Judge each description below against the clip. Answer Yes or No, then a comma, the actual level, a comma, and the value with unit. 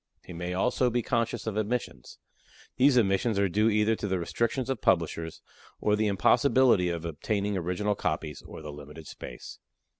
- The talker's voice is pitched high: No, low, 100 Hz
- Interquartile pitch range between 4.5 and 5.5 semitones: Yes, average, 5.2 semitones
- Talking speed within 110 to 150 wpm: No, average, 170 wpm